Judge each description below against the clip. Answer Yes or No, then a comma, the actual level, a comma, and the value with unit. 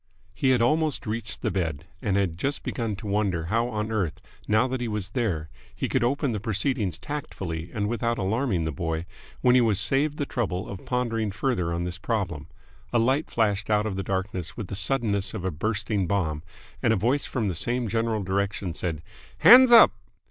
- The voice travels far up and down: No, average, 4.3 semitones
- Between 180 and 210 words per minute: Yes, average, 200 wpm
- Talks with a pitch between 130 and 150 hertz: No, low, 105 Hz